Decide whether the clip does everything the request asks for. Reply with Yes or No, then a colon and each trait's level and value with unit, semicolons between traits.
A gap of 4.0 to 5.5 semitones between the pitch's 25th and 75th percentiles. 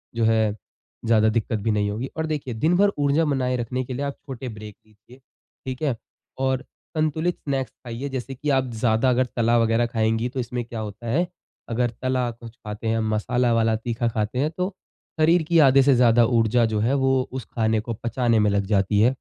No: average, 3.0 semitones